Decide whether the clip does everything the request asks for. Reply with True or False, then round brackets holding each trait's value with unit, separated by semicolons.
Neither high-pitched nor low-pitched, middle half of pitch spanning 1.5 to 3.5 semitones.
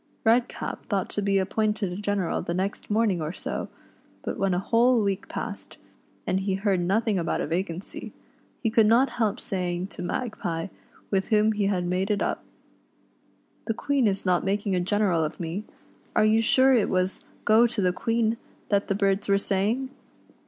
False (200 Hz; 2.9 semitones)